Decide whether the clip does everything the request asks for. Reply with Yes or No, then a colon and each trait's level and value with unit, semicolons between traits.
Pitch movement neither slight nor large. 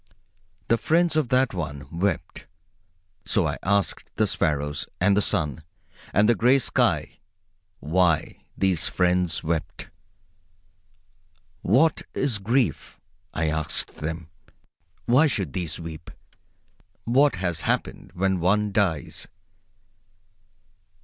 No: wide, 6.2 semitones